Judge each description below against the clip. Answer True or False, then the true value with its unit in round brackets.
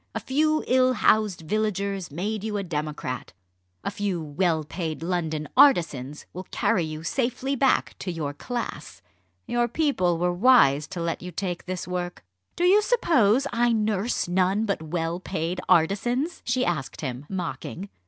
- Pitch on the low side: False (185 Hz)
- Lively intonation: True (6.4 semitones)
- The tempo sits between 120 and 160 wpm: True (155 wpm)